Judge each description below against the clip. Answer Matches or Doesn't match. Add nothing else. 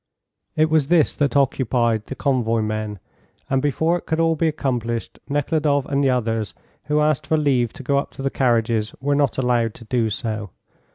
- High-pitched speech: Doesn't match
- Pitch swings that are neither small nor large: Matches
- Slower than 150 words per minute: Doesn't match